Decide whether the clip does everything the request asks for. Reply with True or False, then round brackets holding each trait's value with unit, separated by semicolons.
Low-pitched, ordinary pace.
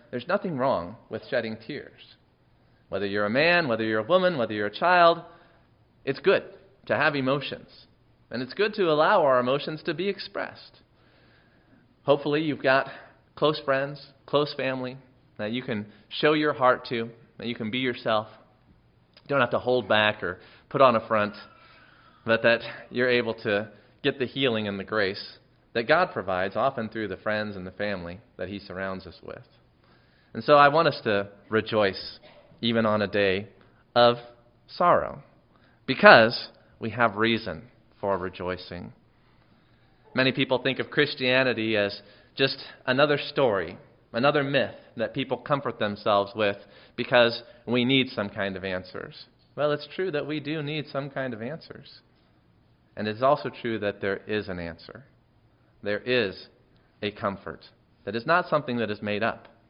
True (115 Hz; 165 wpm)